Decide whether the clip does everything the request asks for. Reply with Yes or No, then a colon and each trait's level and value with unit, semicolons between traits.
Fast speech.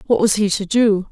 Yes: fast, 270 wpm